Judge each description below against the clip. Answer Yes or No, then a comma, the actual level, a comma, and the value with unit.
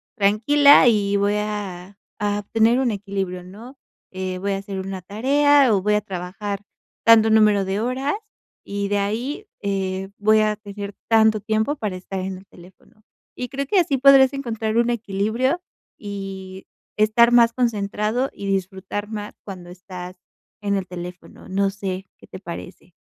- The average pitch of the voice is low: No, high, 205 Hz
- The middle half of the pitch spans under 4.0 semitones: Yes, average, 2.9 semitones